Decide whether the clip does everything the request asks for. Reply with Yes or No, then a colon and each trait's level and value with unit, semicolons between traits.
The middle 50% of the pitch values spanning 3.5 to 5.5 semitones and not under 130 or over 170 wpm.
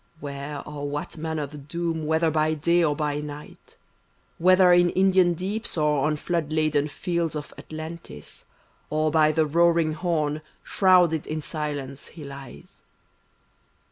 No: narrow, 2.4 semitones; average, 140 wpm